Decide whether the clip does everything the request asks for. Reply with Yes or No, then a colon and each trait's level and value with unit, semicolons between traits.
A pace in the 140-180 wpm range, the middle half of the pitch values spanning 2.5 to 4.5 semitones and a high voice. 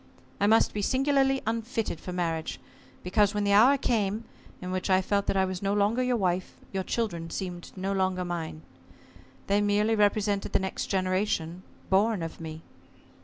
Yes: average, 170 wpm; average, 2.8 semitones; high, 195 Hz